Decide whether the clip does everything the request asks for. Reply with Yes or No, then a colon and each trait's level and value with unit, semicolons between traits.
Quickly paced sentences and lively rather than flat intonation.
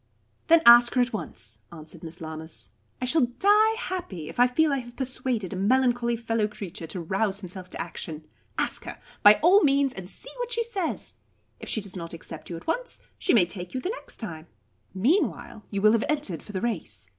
Yes: fast, 210 wpm; wide, 7.6 semitones